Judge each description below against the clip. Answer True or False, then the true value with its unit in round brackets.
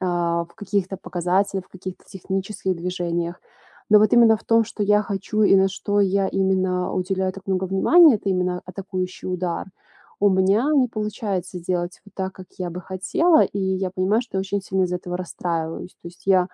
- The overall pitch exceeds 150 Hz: True (190 Hz)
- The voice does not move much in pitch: True (1.8 semitones)